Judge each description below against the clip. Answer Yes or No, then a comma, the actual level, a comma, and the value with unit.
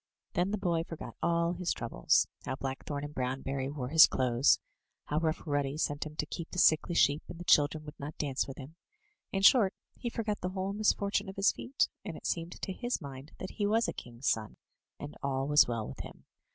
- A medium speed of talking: No, fast, 225 wpm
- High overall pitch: No, medium, 155 Hz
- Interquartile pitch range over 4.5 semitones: Yes, average, 5.2 semitones